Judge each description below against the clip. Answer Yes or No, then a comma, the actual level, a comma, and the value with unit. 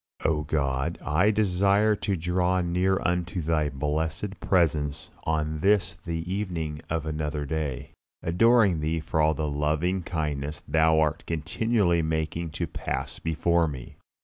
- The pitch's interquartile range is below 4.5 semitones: Yes, average, 2.9 semitones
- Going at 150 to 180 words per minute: No, average, 140 wpm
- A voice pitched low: Yes, very low, 80 Hz